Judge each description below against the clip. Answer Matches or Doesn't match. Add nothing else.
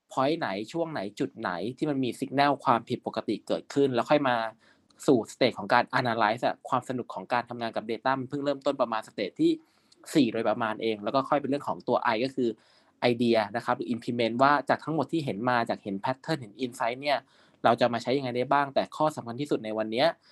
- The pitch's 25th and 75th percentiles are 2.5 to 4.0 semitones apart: Matches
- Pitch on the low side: Matches